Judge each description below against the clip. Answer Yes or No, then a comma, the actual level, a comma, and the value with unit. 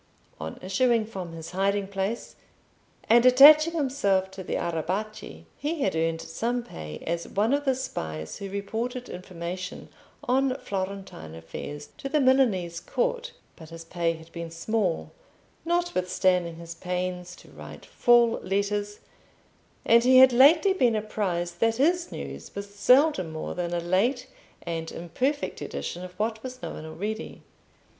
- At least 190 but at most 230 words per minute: No, average, 145 wpm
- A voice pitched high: Yes, high, 200 Hz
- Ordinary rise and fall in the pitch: No, wide, 6.5 semitones